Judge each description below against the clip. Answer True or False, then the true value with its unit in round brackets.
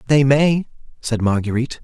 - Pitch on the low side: True (130 Hz)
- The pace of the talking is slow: True (130 wpm)